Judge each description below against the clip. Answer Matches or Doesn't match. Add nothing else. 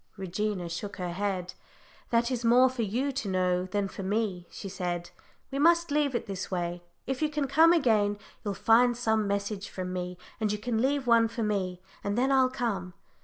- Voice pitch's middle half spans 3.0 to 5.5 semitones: Matches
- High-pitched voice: Matches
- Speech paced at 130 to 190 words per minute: Doesn't match